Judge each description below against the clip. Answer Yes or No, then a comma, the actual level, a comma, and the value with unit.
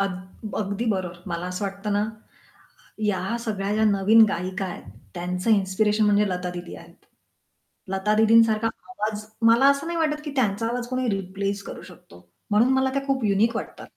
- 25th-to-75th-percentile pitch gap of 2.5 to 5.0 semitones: Yes, average, 3.1 semitones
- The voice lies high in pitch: Yes, high, 210 Hz